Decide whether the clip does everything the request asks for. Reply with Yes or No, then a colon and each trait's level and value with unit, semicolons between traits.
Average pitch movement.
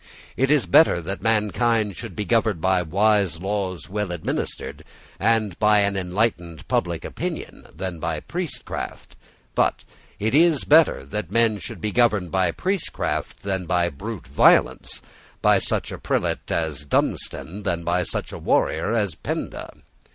Yes: average, 4.1 semitones